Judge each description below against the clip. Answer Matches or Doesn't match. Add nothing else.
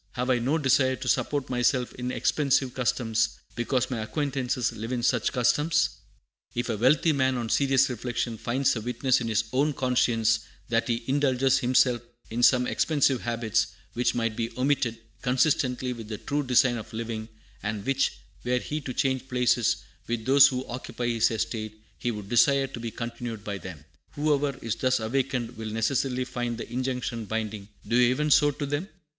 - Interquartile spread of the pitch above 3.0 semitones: Doesn't match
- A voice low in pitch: Matches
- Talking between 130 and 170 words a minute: Doesn't match